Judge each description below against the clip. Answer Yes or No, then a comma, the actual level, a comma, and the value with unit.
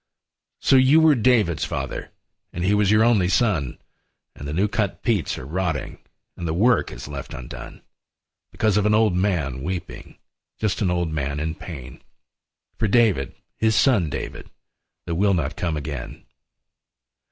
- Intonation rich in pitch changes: Yes, wide, 5.8 semitones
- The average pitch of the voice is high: No, very low, 90 Hz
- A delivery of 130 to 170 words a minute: Yes, average, 160 wpm